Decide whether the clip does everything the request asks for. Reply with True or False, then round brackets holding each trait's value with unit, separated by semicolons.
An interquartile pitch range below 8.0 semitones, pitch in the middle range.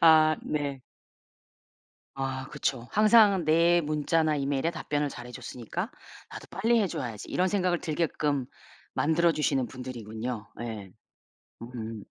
True (5.1 semitones; 145 Hz)